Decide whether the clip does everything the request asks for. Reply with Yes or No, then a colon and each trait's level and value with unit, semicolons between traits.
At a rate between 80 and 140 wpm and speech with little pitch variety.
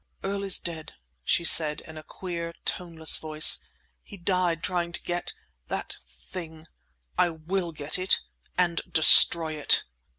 Yes: slow, 135 wpm; narrow, 2.2 semitones